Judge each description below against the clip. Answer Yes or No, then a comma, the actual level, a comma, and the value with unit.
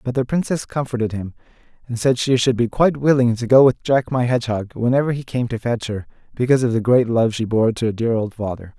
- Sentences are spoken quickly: Yes, fast, 245 wpm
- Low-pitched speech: Yes, low, 120 Hz